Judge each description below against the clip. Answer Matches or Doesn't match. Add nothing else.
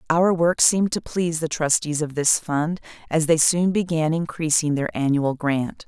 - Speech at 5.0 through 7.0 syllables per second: Doesn't match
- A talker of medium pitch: Matches